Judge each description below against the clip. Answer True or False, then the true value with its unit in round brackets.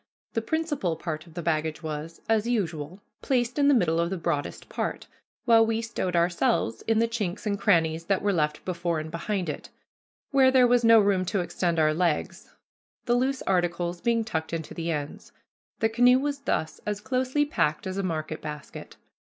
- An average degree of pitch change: False (6.1 semitones)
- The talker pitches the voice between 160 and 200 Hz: True (185 Hz)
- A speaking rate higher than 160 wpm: True (190 wpm)